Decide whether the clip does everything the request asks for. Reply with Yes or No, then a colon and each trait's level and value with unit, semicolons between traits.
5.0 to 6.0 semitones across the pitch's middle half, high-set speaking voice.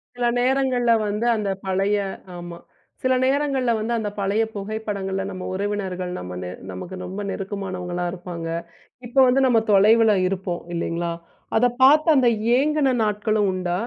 No: average, 4.6 semitones; high, 205 Hz